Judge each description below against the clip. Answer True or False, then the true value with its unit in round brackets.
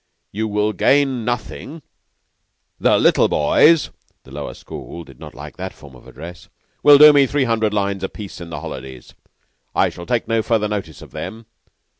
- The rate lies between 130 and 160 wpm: False (175 wpm)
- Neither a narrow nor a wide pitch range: False (6.4 semitones)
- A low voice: True (105 Hz)